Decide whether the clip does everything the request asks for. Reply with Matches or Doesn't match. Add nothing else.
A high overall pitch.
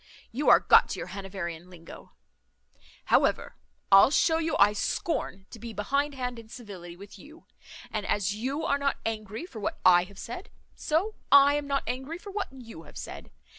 Matches